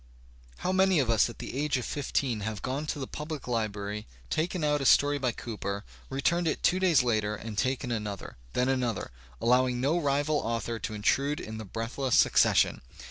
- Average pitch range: Yes, average, 4.8 semitones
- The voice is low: Yes, low, 130 Hz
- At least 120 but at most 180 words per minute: No, average, 190 wpm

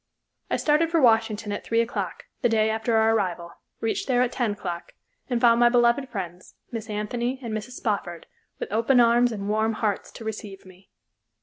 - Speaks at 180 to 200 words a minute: Yes, average, 190 wpm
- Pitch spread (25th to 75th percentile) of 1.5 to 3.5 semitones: Yes, narrow, 2.6 semitones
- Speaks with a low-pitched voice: No, high, 225 Hz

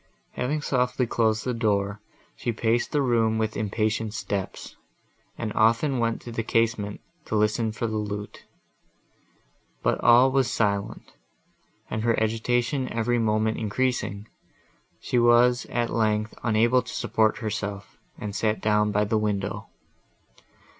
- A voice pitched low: Yes, low, 110 Hz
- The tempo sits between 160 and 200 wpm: No, slow, 135 wpm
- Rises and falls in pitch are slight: Yes, narrow, 2.0 semitones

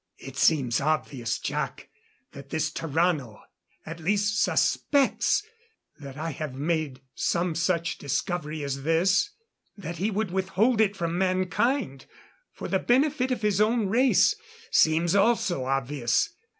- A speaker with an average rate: No, slow, 130 wpm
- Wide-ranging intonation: Yes, wide, 6.0 semitones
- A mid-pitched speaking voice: Yes, medium, 170 Hz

